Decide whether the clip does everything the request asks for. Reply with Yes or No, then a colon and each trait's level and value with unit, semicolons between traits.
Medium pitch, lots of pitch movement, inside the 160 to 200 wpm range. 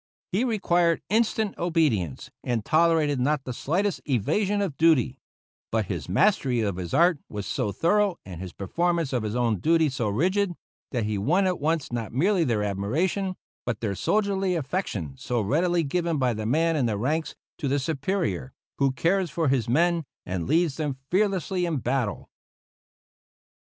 Yes: medium, 150 Hz; wide, 7.3 semitones; average, 165 wpm